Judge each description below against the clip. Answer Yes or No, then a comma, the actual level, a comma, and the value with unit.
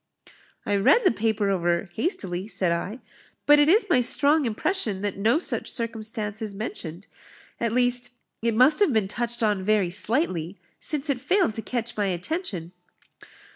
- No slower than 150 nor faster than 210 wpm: Yes, average, 165 wpm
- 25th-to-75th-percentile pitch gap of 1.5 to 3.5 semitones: No, average, 4.7 semitones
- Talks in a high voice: Yes, high, 220 Hz